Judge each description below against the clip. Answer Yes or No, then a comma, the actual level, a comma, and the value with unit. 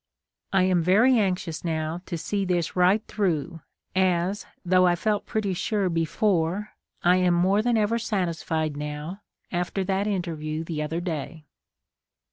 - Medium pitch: Yes, medium, 180 Hz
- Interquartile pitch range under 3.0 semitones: No, average, 3.4 semitones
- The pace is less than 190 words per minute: Yes, average, 145 wpm